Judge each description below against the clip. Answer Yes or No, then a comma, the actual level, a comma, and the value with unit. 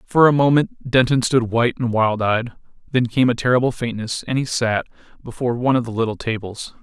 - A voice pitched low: Yes, low, 120 Hz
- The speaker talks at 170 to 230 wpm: Yes, average, 200 wpm